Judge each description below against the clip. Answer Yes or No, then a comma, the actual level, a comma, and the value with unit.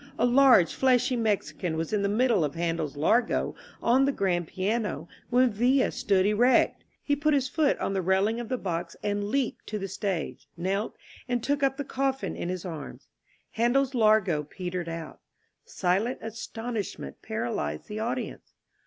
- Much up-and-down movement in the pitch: Yes, wide, 5.7 semitones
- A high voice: Yes, high, 215 Hz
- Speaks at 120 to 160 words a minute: No, average, 170 wpm